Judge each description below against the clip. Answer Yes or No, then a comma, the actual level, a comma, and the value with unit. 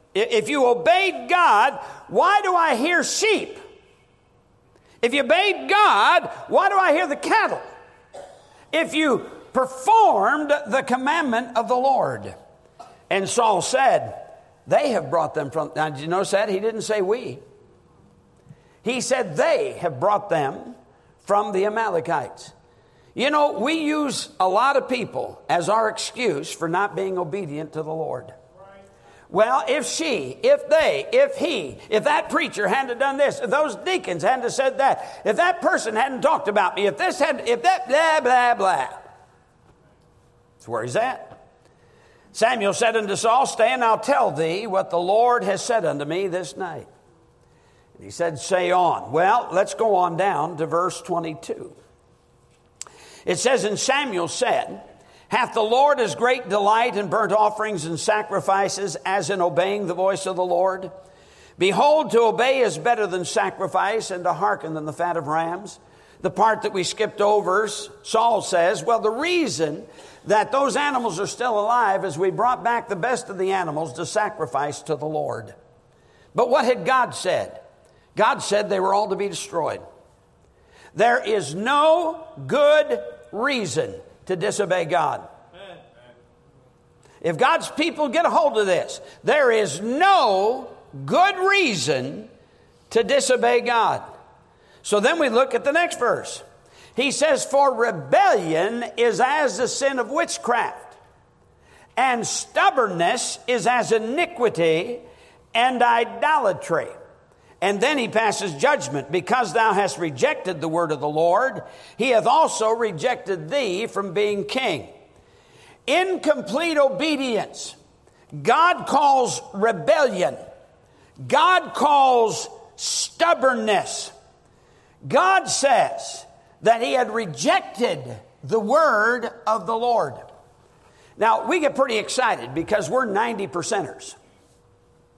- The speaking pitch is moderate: No, high, 230 Hz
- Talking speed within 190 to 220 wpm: No, average, 145 wpm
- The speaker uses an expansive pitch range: Yes, wide, 7.3 semitones